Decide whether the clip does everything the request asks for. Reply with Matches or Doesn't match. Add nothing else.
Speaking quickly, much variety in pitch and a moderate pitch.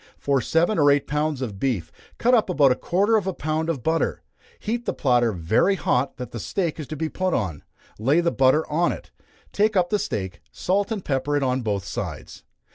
Matches